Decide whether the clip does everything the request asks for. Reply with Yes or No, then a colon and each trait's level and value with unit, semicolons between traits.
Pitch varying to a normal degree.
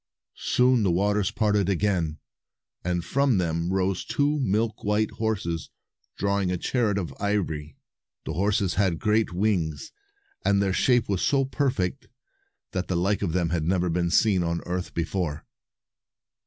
Yes: average, 3.5 semitones